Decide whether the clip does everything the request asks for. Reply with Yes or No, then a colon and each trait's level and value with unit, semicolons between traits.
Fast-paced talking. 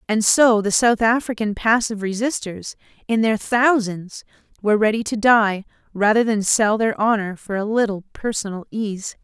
No: average, 155 wpm